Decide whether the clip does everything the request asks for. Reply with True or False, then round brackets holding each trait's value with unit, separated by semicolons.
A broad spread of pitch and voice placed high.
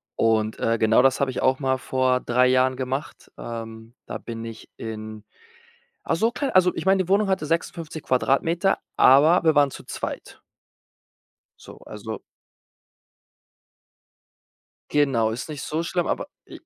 False (6.1 semitones; 130 Hz)